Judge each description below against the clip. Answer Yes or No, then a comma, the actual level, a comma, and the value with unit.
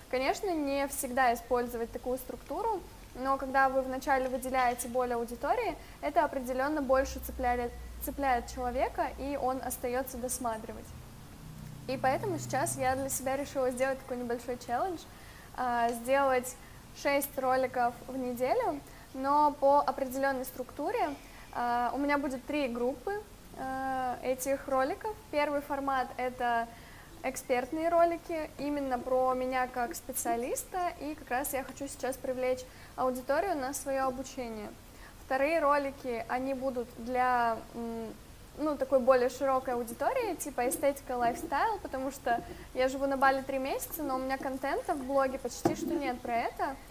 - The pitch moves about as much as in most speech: No, narrow, 1.9 semitones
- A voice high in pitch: Yes, very high, 265 Hz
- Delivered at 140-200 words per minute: No, average, 130 wpm